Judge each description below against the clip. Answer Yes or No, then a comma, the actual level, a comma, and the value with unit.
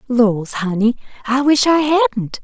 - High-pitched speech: Yes, high, 240 Hz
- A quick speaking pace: No, average, 150 wpm